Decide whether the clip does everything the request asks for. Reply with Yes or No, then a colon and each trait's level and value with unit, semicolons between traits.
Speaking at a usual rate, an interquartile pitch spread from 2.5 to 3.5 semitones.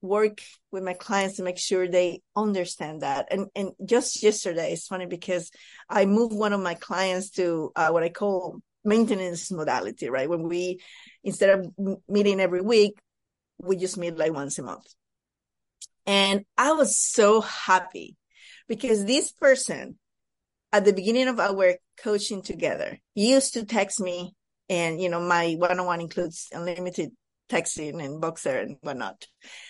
Yes: average, 160 wpm; average, 2.9 semitones